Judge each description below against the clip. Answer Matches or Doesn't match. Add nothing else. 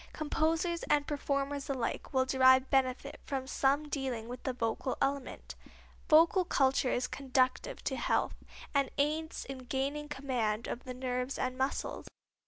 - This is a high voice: Matches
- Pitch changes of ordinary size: Doesn't match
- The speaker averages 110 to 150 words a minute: Matches